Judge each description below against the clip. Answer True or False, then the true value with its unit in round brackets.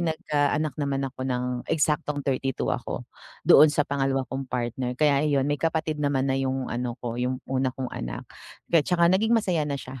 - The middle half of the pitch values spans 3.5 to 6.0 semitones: False (2.6 semitones)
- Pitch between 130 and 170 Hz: True (140 Hz)